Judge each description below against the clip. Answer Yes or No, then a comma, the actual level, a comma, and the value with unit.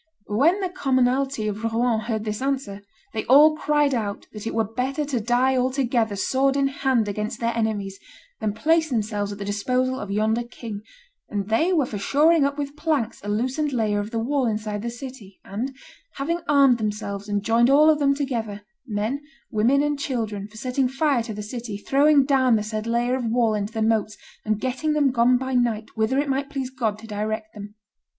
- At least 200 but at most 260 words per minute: Yes, fast, 205 wpm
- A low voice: No, high, 240 Hz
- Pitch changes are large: No, average, 4.2 semitones